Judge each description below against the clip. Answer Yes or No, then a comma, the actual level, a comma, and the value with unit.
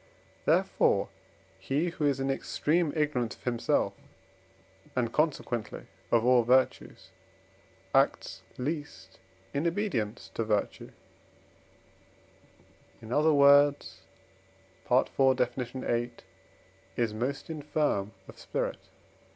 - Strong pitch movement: No, average, 3.9 semitones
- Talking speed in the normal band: No, slow, 95 wpm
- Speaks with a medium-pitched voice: No, low, 130 Hz